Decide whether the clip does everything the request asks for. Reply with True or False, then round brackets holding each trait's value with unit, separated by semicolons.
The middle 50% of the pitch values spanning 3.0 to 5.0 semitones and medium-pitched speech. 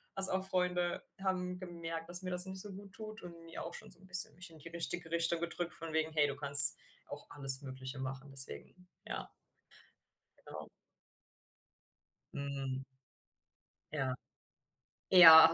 True (4.1 semitones; 165 Hz)